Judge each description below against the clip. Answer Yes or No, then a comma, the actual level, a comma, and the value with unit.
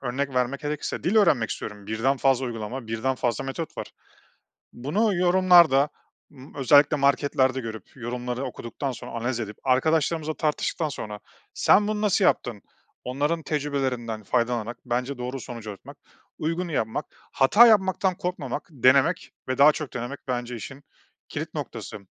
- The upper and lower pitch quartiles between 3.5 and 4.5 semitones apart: Yes, average, 4.0 semitones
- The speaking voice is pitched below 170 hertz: Yes, low, 135 Hz